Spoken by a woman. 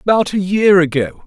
No: male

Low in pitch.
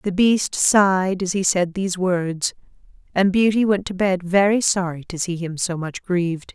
No: medium, 185 Hz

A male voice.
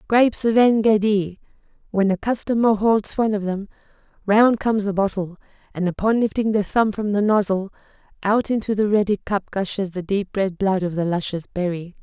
No: female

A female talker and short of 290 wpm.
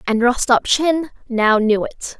Yes: female; slow, 135 wpm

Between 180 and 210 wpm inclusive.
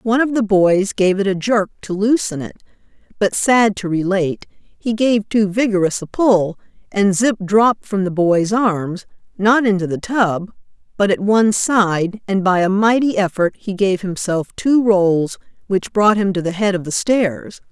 Yes: average, 185 wpm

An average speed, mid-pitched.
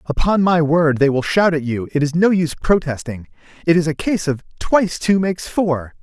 No: fast, 220 wpm; medium, 160 Hz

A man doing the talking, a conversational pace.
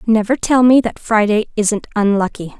No: female; average, 160 wpm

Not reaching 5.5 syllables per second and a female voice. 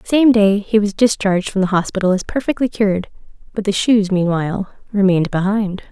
No: 5.8 syllables/s; female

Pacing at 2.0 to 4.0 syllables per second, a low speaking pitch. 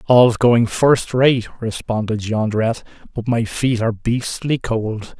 Yes: 3.8 syllables/s; low, 115 Hz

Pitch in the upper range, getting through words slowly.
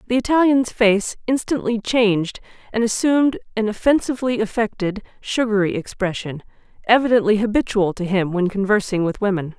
Yes: high, 215 Hz; slow, 125 wpm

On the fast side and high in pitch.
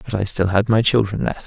No: fast, 285 wpm; low, 105 Hz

